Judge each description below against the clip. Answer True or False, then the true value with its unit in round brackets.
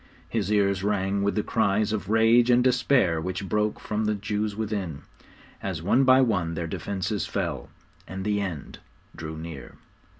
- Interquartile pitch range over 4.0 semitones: False (2.8 semitones)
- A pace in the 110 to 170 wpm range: True (165 wpm)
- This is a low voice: True (100 Hz)